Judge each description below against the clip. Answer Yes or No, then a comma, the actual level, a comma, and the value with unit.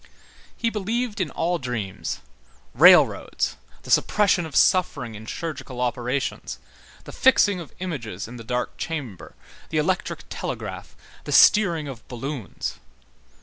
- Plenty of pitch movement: Yes, wide, 7.1 semitones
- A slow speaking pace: Yes, slow, 125 wpm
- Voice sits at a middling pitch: Yes, medium, 150 Hz